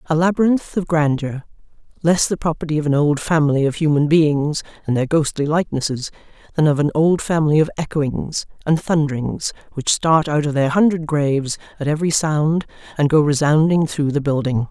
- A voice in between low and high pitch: Yes, medium, 155 Hz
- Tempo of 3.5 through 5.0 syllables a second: No, 5.4 syllables/s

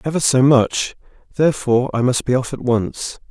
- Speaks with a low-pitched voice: Yes, low, 130 Hz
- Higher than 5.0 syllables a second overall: Yes, 5.2 syllables/s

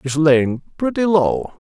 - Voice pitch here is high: No, medium, 160 Hz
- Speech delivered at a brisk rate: No, average, 145 wpm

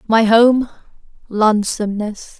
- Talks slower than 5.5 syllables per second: Yes, 4.2 syllables/s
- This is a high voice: Yes, high, 220 Hz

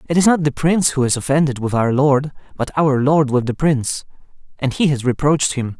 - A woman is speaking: No, male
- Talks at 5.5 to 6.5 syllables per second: Yes, 5.8 syllables/s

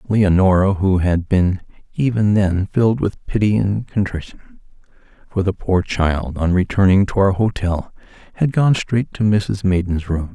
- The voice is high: No, very low, 95 Hz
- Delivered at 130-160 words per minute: Yes, average, 155 wpm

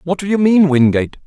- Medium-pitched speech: Yes, medium, 165 Hz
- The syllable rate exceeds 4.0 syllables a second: Yes, 6.3 syllables/s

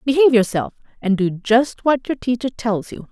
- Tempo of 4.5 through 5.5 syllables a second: Yes, 5.1 syllables/s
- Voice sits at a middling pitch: No, high, 235 Hz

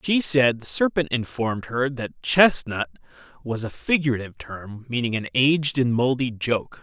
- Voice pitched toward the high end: No, low, 125 Hz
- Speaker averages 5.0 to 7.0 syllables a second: No, 4.8 syllables/s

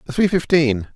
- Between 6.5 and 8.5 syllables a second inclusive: No, 5.1 syllables/s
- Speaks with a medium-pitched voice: Yes, medium, 150 Hz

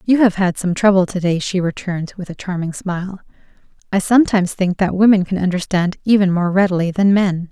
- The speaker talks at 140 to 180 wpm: No, average, 200 wpm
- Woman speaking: Yes, female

